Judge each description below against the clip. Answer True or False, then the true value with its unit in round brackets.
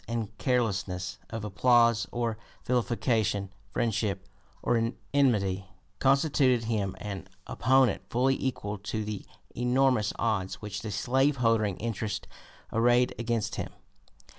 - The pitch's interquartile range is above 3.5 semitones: False (3.2 semitones)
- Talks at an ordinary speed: False (115 wpm)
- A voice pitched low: True (115 Hz)